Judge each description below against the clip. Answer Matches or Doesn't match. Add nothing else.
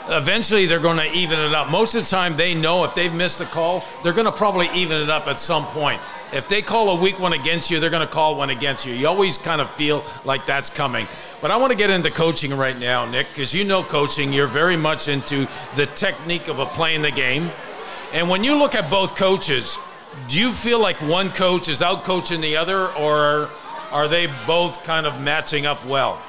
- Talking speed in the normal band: Doesn't match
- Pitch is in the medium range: Matches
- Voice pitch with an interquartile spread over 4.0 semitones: Doesn't match